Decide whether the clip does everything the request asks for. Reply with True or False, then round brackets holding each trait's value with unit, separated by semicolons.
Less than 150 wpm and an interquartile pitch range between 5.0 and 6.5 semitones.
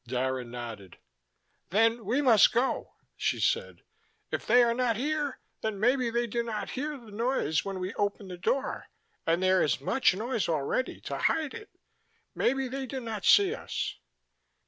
False (170 wpm; 5.5 semitones)